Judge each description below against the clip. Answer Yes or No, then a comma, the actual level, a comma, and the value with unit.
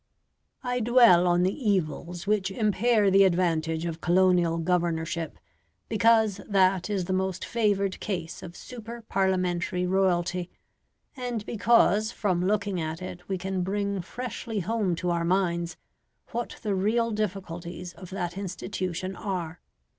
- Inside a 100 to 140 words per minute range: Yes, slow, 135 wpm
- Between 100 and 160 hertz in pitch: No, high, 190 Hz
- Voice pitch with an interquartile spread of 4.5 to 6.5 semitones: No, average, 3.1 semitones